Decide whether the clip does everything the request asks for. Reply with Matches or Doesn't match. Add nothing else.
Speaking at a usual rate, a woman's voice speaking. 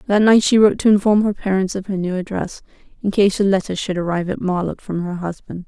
Doesn't match